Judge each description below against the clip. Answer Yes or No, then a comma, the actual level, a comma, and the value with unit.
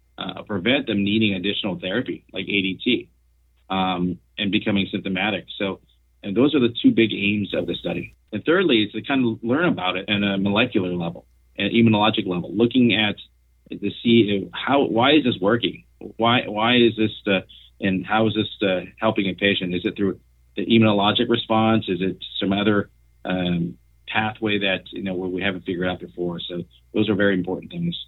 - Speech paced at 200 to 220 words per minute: No, average, 185 wpm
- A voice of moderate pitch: No, low, 100 Hz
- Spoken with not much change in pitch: No, average, 3.3 semitones